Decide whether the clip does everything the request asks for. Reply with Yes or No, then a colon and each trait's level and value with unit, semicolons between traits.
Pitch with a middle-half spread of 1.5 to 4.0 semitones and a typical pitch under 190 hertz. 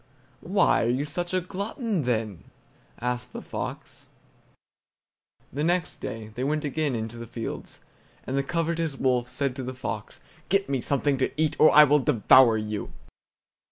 No: average, 4.4 semitones; low, 135 Hz